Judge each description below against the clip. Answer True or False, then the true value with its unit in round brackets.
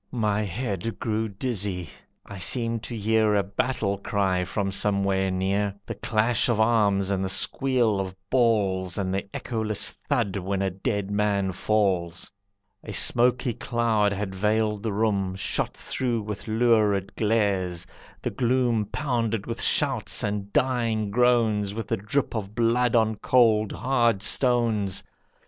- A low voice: True (105 Hz)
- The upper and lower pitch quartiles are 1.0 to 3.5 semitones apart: True (2.8 semitones)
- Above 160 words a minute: False (145 wpm)